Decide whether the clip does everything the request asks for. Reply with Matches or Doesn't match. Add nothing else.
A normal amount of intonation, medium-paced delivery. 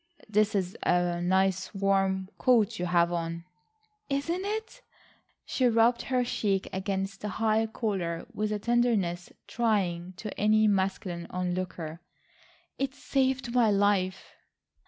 Doesn't match